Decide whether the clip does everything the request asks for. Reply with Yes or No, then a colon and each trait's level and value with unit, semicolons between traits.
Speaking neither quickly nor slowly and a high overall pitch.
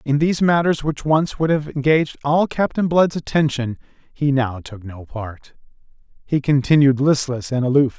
No: average, 165 wpm; medium, 140 Hz